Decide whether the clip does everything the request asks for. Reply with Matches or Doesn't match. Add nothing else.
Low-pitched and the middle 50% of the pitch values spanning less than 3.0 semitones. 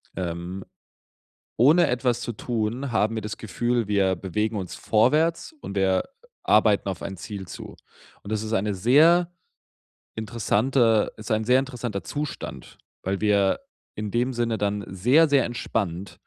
Doesn't match